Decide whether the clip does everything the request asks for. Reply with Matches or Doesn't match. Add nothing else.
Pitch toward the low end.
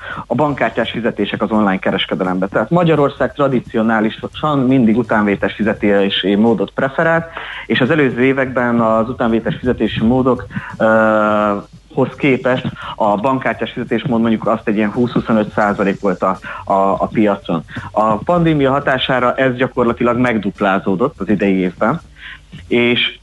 Matches